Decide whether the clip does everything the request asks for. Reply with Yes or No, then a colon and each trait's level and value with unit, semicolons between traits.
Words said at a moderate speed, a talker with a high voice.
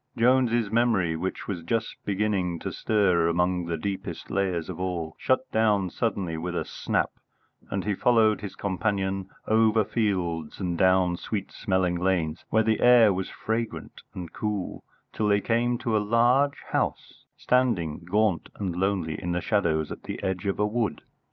No: average, 165 wpm; low, 100 Hz